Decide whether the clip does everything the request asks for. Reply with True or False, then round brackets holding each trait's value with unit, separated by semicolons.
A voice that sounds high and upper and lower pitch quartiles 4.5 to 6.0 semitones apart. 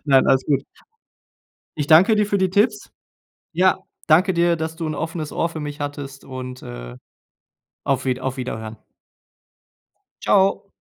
False (155 Hz; 5.2 semitones)